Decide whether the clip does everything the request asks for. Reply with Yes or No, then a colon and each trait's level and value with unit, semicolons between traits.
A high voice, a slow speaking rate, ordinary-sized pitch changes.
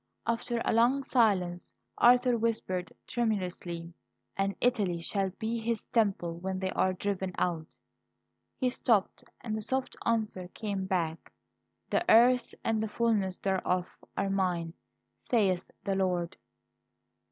Yes: high, 195 Hz; slow, 130 wpm; average, 4.1 semitones